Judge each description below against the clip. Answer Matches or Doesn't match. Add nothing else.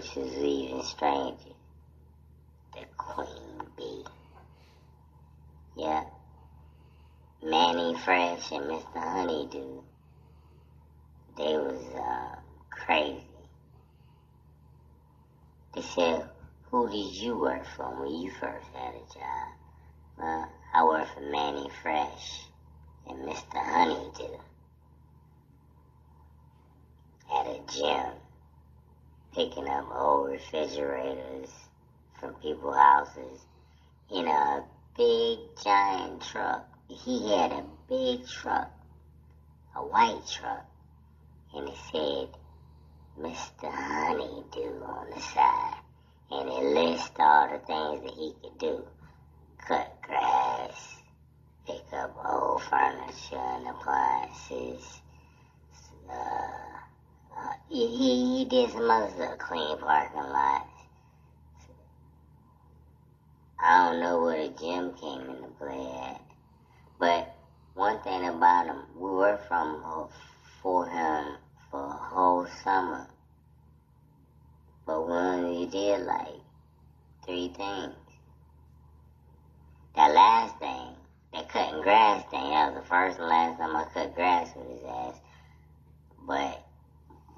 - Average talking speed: Doesn't match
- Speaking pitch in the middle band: Doesn't match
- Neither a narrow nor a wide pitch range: Matches